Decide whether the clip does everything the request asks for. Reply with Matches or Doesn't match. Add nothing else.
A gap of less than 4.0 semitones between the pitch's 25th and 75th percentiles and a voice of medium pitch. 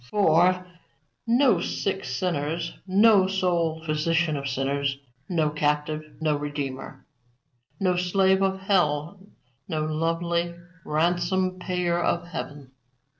Matches